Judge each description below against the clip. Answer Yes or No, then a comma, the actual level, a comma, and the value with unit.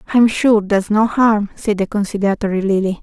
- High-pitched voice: Yes, high, 210 Hz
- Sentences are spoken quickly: No, average, 180 wpm